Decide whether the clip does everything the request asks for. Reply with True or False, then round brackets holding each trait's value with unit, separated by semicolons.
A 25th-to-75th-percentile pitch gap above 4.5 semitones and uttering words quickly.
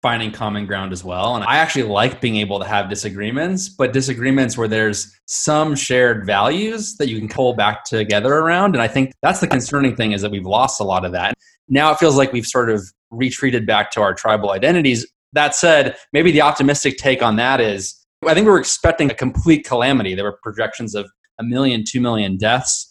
True (5.0 semitones; 215 wpm)